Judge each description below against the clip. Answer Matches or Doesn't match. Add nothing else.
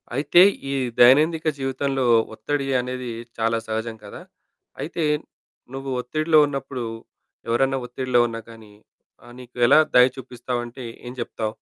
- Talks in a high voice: Doesn't match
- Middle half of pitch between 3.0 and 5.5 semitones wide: Doesn't match